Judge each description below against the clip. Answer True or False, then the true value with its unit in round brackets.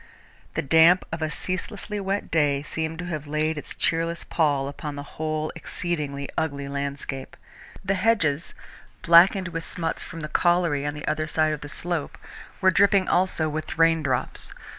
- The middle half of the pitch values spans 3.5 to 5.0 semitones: False (2.9 semitones)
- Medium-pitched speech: True (160 Hz)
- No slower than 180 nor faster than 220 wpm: False (160 wpm)